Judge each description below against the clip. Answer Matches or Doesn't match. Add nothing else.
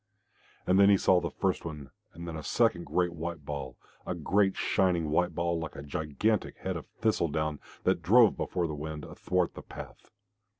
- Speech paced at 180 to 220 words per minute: Matches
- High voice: Doesn't match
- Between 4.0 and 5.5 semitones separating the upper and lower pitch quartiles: Doesn't match